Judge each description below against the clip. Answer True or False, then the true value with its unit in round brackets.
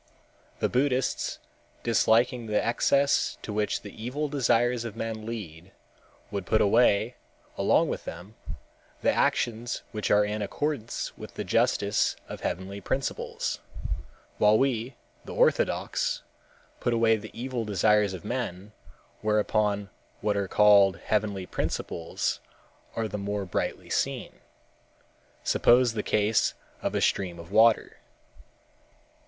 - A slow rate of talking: True (125 wpm)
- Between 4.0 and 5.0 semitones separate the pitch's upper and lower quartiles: False (2.8 semitones)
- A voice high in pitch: False (110 Hz)